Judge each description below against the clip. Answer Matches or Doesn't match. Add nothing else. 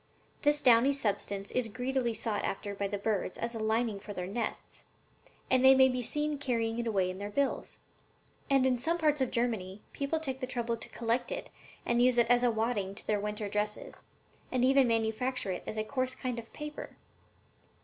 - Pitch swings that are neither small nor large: Matches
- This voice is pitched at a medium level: Doesn't match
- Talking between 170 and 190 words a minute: Doesn't match